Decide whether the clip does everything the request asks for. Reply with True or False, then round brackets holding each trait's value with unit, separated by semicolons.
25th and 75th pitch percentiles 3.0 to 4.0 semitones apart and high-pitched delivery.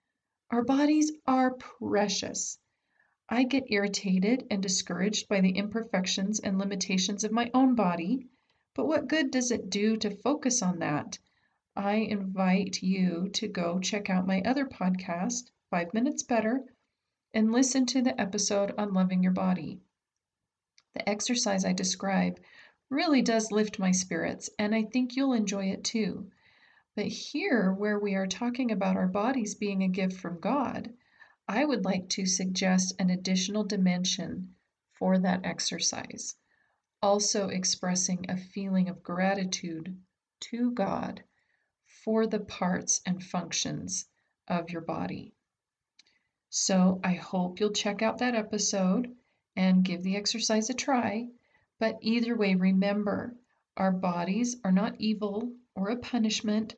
True (3.7 semitones; 205 Hz)